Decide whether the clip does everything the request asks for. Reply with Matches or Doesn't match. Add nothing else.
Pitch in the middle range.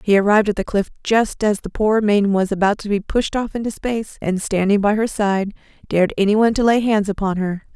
Doesn't match